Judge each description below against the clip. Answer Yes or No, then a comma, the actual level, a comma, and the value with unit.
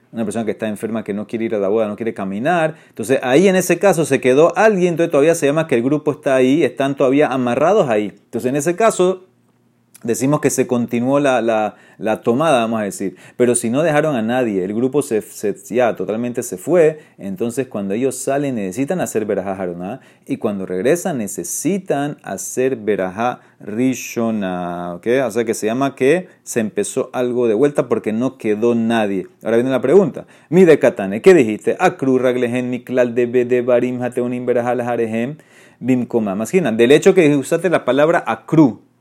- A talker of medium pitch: No, low, 125 Hz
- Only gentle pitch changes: No, average, 3.7 semitones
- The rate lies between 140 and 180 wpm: Yes, average, 175 wpm